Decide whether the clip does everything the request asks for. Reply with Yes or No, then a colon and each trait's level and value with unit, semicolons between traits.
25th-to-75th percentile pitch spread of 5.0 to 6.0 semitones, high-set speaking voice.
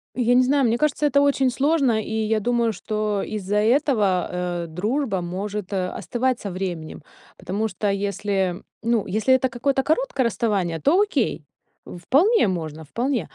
Yes: average, 5.3 semitones; high, 220 Hz